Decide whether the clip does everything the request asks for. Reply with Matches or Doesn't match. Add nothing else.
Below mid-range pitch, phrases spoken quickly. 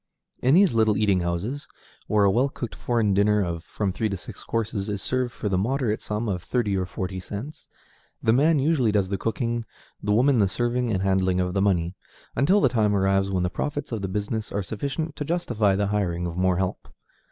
Matches